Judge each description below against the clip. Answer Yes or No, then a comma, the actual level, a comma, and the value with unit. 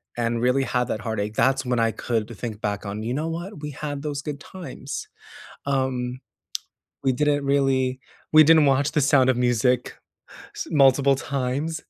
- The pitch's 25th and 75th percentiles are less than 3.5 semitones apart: Yes, average, 2.9 semitones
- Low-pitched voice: Yes, low, 130 Hz